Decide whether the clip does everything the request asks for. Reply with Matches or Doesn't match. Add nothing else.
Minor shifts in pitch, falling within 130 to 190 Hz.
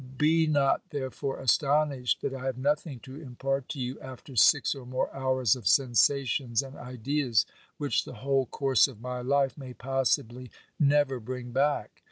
Matches